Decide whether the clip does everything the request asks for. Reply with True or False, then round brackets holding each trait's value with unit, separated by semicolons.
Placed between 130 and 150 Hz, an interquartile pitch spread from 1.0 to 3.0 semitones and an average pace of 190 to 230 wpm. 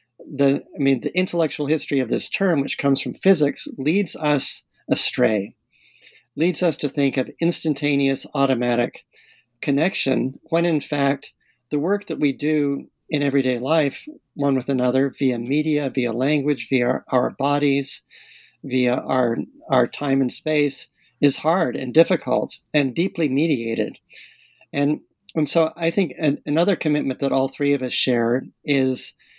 False (140 Hz; 2.7 semitones; 150 wpm)